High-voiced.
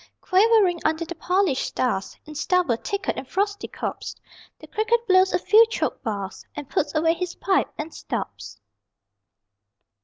Yes: very high, 360 Hz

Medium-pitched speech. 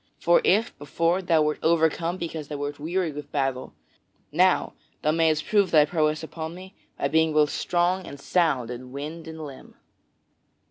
Yes: medium, 160 Hz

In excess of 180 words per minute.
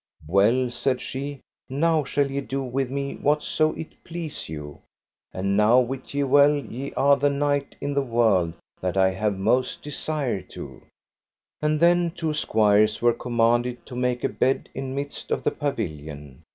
No: average, 165 wpm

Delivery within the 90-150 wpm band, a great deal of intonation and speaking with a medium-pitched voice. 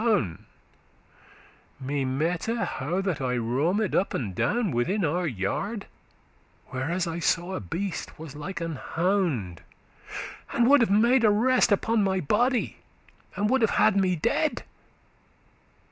Yes: average, 145 wpm; wide, 6.4 semitones; medium, 180 Hz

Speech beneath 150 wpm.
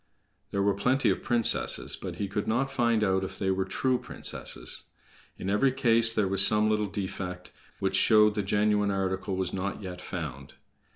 No: average, 180 wpm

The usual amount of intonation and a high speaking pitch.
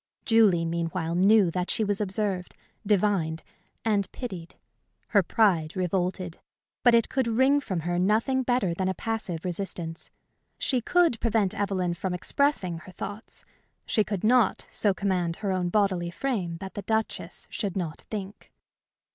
Yes: average, 3.9 semitones; high, 195 Hz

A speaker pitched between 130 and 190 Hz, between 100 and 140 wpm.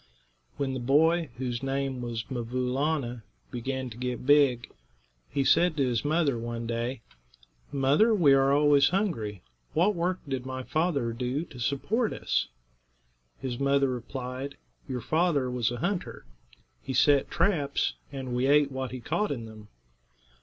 No: low, 135 Hz; average, 155 wpm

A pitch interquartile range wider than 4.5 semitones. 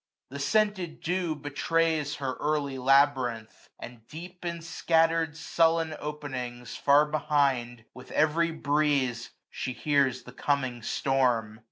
No: average, 4.0 semitones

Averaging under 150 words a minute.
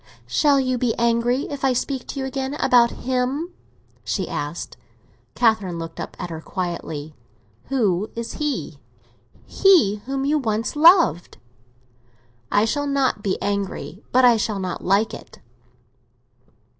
Yes: average, 140 wpm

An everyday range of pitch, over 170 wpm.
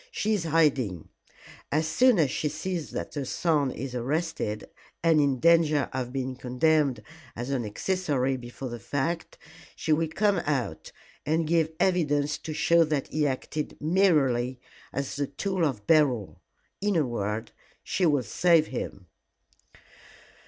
No: average, 4.2 semitones; average, 145 wpm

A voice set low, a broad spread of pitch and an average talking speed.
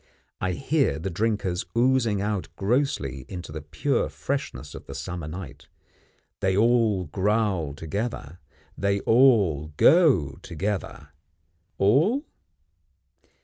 No: low, 100 Hz; wide, 6.2 semitones; slow, 105 wpm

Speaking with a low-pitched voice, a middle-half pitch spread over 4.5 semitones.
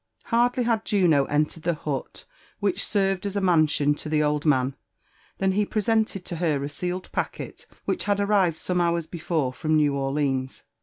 No: medium, 170 Hz; average, 5.1 semitones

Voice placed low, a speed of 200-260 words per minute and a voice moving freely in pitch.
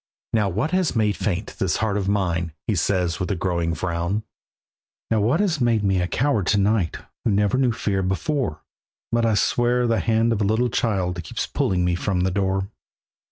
No: low, 100 Hz; fast, 205 wpm; average, 3.9 semitones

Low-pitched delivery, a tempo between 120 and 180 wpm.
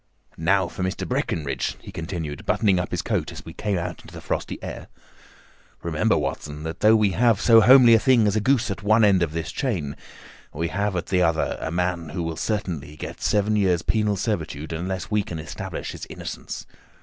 No: very low, 95 Hz; fast, 205 wpm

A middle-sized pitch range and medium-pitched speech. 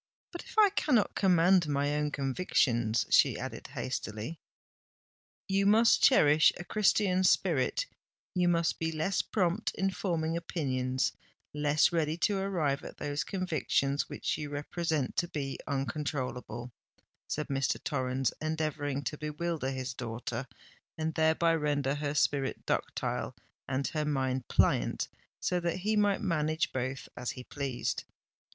Yes: average, 4.4 semitones; medium, 150 Hz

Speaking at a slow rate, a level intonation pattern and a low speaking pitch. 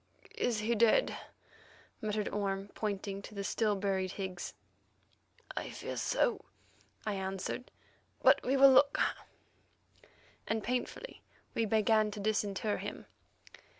No: slow, 110 wpm; narrow, 2.3 semitones; high, 210 Hz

